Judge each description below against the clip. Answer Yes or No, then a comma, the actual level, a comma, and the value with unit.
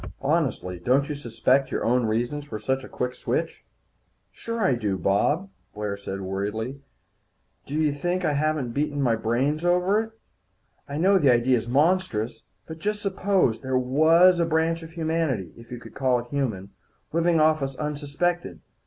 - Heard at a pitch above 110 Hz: Yes, medium, 140 Hz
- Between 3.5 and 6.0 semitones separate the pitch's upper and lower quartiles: Yes, wide, 5.5 semitones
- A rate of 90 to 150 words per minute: No, average, 170 wpm